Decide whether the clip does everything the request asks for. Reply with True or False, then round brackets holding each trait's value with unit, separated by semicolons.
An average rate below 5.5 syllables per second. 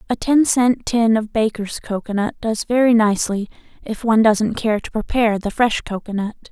True (5.1 syllables/s)